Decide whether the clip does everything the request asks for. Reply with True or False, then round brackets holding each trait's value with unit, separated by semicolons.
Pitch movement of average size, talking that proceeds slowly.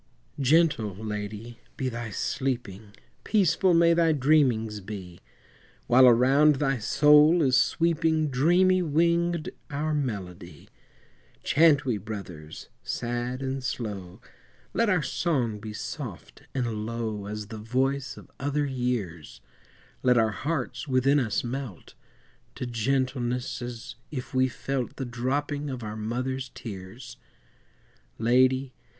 True (4.7 semitones; 120 wpm)